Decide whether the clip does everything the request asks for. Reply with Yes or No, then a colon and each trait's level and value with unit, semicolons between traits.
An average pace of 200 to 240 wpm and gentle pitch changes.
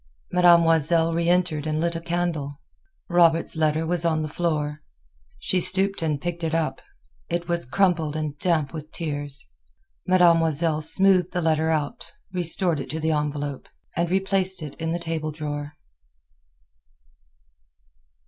No: average, 140 wpm; narrow, 2.2 semitones